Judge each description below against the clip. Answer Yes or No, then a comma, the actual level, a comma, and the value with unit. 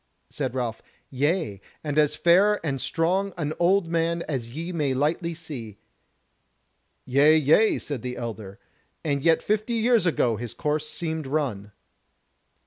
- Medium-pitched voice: Yes, medium, 155 Hz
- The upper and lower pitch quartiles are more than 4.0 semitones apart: Yes, average, 4.7 semitones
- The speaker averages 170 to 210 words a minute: No, average, 140 wpm